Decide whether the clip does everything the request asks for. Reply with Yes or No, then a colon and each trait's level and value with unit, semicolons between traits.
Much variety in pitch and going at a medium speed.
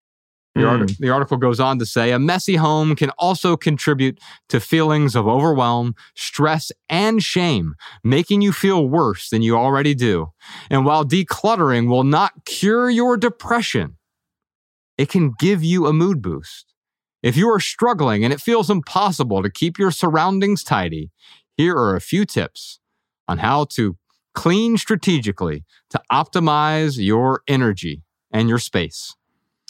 Yes: wide, 7.4 semitones; average, 150 wpm